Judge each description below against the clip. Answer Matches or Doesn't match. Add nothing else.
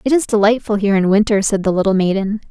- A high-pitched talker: Matches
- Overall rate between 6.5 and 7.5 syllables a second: Matches